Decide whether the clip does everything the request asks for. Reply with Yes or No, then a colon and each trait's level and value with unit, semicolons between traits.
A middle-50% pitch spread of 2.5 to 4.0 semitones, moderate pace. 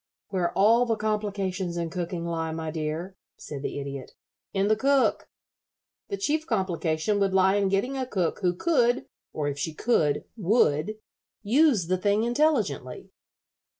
No: wide, 5.5 semitones; average, 150 wpm